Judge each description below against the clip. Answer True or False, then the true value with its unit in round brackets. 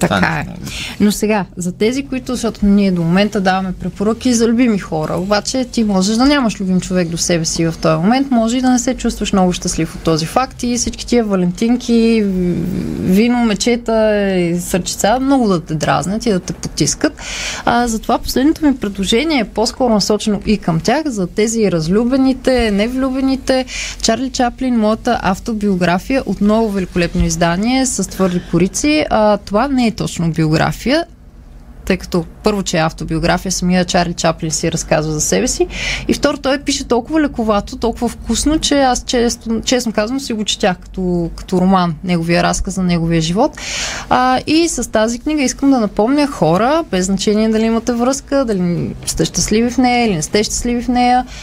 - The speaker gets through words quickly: True (175 wpm)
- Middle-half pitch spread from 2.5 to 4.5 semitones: False (5.2 semitones)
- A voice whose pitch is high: True (215 Hz)